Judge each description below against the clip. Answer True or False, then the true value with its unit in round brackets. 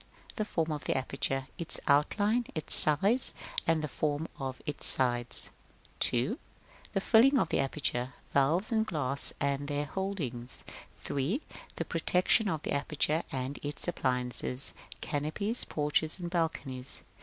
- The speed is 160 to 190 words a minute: False (150 wpm)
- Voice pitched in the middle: True (150 Hz)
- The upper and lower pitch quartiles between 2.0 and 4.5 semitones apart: False (4.9 semitones)